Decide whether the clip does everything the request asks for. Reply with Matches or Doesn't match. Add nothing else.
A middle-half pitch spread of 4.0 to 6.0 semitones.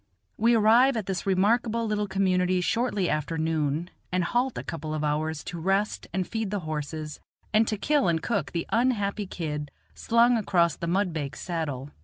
Matches